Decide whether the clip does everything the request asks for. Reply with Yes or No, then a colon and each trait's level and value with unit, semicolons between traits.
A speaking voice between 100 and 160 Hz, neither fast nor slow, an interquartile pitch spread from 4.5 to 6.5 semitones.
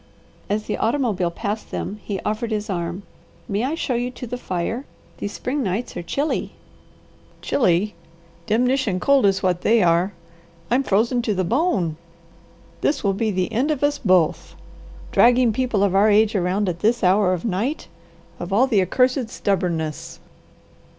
No: high, 210 Hz; average, 165 wpm; average, 4.9 semitones